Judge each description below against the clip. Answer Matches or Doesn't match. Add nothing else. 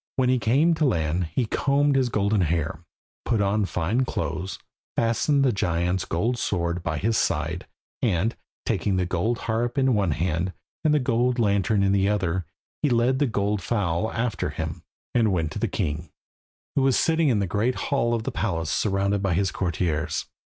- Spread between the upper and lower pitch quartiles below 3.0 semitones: Doesn't match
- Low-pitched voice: Matches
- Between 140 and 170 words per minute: Doesn't match